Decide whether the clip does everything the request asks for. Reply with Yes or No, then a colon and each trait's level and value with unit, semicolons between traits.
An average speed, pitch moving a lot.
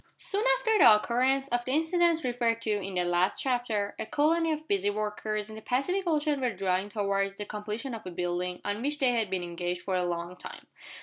No: fast, 220 wpm; wide, 5.9 semitones